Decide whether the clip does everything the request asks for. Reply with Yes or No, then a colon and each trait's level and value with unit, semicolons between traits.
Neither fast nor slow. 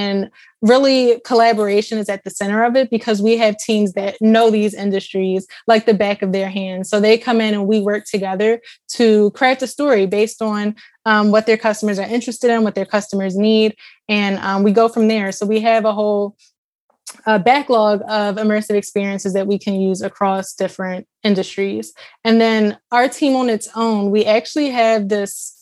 Yes: average, 190 wpm